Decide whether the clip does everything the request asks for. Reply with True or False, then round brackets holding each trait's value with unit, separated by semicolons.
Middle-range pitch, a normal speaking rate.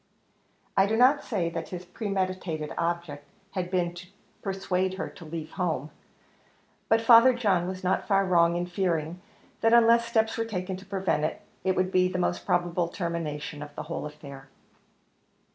True (180 Hz; 175 wpm)